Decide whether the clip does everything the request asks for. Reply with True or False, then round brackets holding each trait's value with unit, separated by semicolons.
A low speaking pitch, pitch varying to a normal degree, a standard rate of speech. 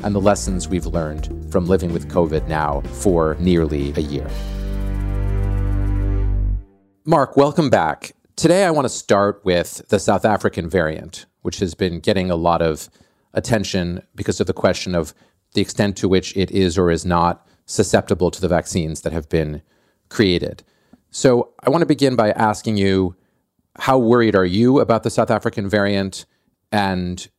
True (95 Hz; 3.1 semitones; 165 wpm)